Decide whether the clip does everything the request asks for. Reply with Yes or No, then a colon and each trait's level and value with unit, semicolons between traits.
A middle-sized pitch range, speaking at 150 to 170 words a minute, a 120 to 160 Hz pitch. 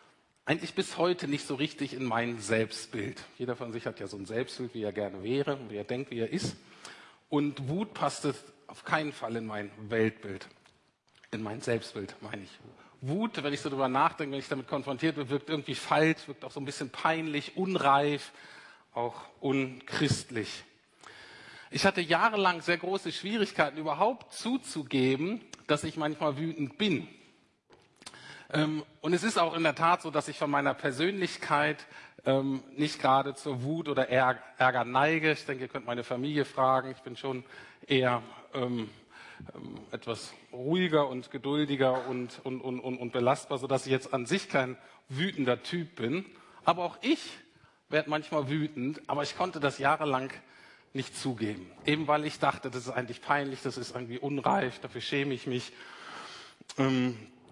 Yes: average, 3.5 semitones; average, 165 wpm; medium, 140 Hz